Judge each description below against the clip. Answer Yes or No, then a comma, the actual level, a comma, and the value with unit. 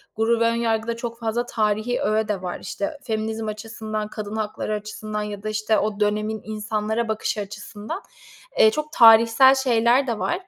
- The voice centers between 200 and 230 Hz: Yes, high, 220 Hz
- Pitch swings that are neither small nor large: No, narrow, 1.5 semitones